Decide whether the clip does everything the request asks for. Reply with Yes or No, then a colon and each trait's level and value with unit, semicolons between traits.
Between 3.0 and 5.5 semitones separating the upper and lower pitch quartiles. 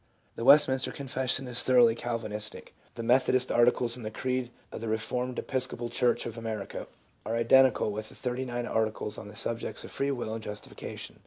No: narrow, 2.4 semitones